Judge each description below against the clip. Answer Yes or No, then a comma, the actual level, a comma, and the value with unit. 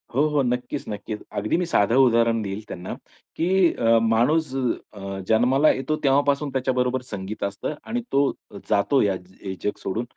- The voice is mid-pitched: No, low, 120 Hz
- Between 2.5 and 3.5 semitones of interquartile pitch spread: No, average, 4.6 semitones